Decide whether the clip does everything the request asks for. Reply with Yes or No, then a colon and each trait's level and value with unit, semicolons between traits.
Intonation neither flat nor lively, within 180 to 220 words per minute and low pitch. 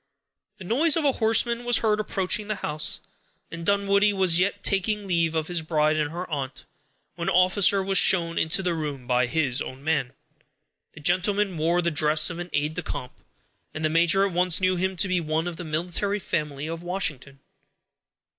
No: average, 3.9 semitones; average, 195 wpm; medium, 175 Hz